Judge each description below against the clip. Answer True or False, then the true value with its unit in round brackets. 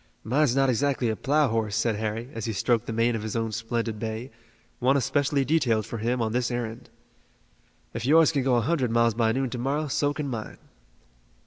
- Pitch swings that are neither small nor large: True (3.2 semitones)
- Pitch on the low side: True (120 Hz)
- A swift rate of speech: True (210 wpm)